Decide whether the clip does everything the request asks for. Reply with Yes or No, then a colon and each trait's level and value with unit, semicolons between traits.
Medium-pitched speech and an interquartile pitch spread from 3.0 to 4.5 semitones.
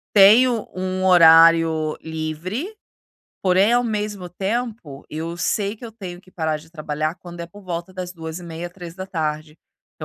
Yes: medium, 175 Hz; average, 3.5 semitones